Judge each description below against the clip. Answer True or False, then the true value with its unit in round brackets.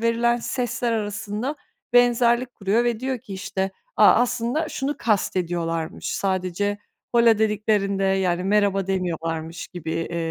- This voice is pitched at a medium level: False (205 Hz)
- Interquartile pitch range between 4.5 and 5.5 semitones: False (4.1 semitones)